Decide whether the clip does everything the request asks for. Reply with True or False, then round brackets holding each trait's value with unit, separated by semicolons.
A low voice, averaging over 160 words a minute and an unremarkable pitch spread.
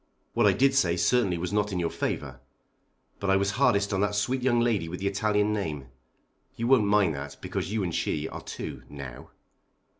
True (100 Hz; 205 wpm; 4.1 semitones)